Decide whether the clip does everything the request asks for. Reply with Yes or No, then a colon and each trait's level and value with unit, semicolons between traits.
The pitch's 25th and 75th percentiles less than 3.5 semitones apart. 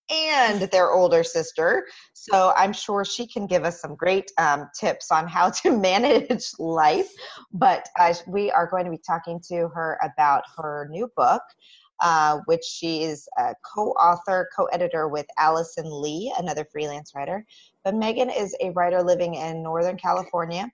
No: average, 5.2 semitones